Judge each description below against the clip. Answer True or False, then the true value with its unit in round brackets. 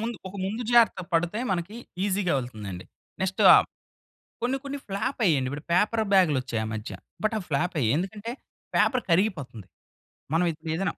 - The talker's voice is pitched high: False (180 Hz)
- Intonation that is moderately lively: False (6.8 semitones)